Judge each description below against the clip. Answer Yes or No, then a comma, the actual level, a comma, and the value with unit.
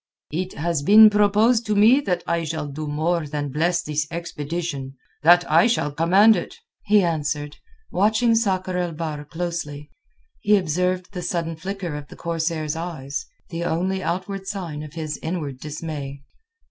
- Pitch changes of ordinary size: Yes, average, 3.7 semitones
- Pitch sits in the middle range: Yes, medium, 170 Hz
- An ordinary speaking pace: Yes, average, 155 wpm